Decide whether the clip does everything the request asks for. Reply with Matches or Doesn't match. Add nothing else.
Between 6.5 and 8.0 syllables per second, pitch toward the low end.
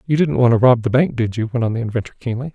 Matches